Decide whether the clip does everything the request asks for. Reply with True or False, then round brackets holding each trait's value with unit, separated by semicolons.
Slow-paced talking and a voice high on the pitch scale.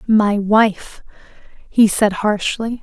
True (105 wpm; 210 Hz)